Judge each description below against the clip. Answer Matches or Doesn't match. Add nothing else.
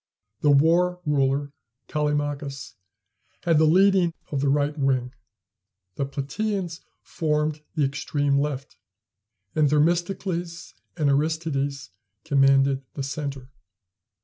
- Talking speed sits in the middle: Doesn't match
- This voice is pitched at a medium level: Matches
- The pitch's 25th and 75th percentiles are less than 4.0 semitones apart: Matches